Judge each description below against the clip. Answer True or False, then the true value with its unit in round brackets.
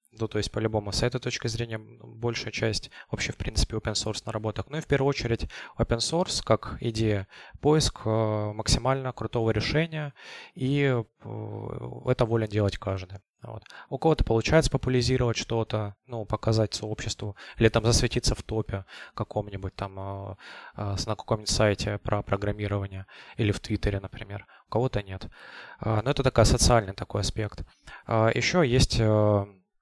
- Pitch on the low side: True (110 Hz)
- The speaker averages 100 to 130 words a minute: False (145 wpm)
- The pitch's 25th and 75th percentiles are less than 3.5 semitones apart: True (2.9 semitones)